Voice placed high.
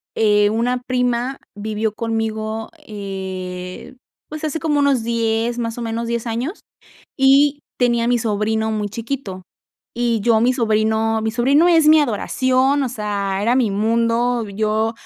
Yes: high, 230 Hz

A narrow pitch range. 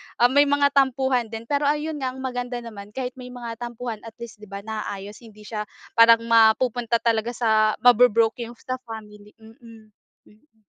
Yes: narrow, 2.3 semitones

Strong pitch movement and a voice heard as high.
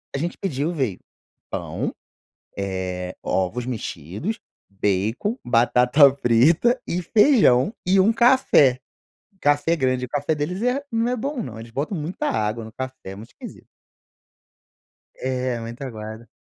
No: wide, 7.9 semitones; low, 130 Hz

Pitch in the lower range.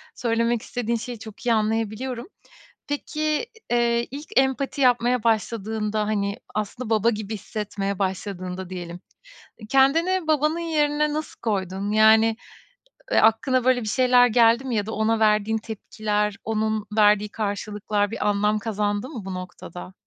No: high, 220 Hz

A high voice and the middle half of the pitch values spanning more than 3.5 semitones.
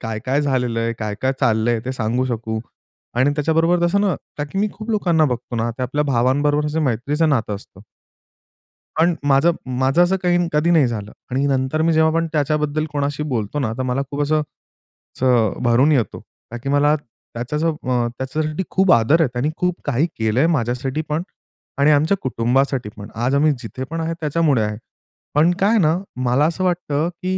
No: medium, 140 Hz; average, 4.5 semitones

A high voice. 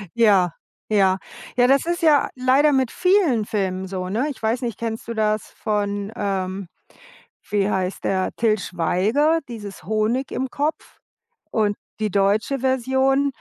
Yes: high, 220 Hz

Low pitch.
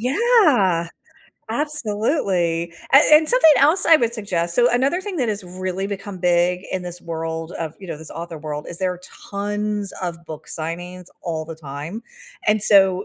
No: medium, 185 Hz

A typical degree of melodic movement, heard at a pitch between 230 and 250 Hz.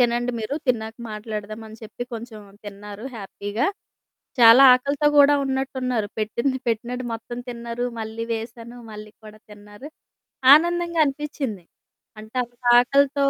Yes: average, 3.3 semitones; high, 235 Hz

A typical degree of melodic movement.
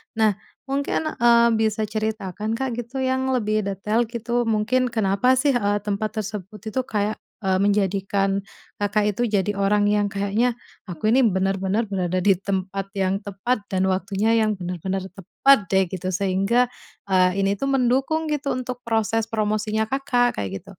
Yes: average, 3.4 semitones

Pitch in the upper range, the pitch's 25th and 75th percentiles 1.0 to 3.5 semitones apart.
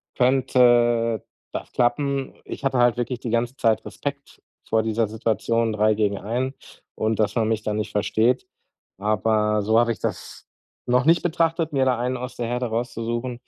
No: low, 120 Hz; narrow, 2.4 semitones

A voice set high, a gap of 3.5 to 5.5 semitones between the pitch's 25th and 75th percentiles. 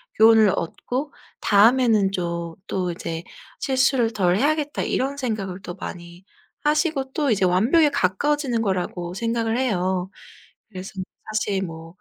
No: high, 215 Hz; wide, 6.3 semitones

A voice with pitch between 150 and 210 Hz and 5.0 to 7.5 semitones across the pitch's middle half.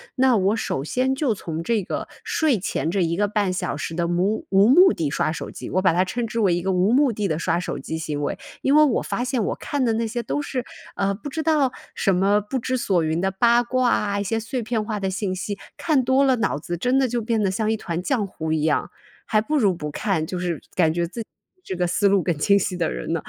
Yes: high, 200 Hz; wide, 5.4 semitones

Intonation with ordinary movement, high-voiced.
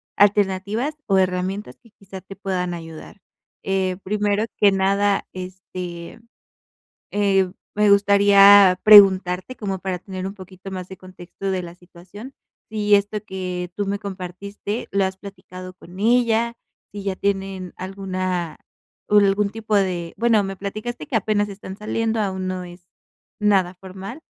No: narrow, 1.8 semitones; high, 195 Hz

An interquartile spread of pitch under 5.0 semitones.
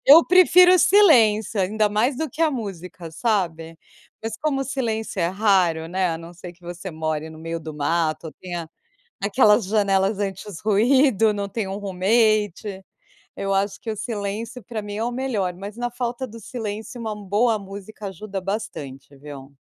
Yes: average, 4.1 semitones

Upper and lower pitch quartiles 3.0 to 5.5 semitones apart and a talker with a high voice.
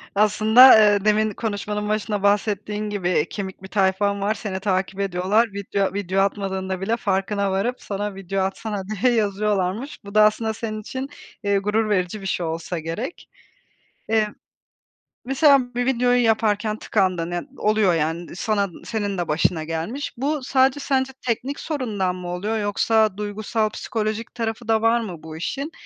No: narrow, 2.6 semitones; high, 210 Hz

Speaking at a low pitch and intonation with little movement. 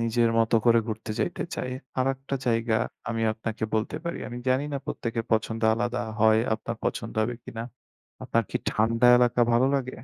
Yes: low, 115 Hz; narrow, 1.8 semitones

